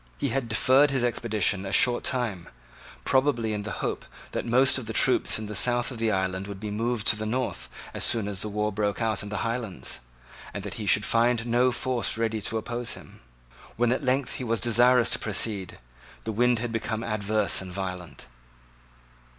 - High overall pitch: No, low, 115 Hz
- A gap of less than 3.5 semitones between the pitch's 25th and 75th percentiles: Yes, average, 2.9 semitones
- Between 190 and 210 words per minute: Yes, average, 200 wpm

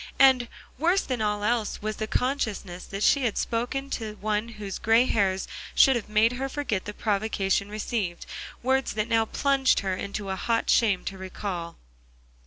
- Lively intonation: No, average, 3.5 semitones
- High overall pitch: Yes, high, 215 Hz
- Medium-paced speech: Yes, average, 175 wpm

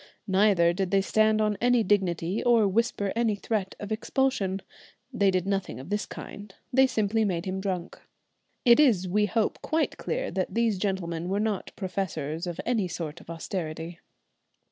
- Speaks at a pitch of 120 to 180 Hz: No, high, 195 Hz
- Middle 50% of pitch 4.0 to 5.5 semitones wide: No, average, 3.2 semitones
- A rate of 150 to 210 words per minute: Yes, average, 165 wpm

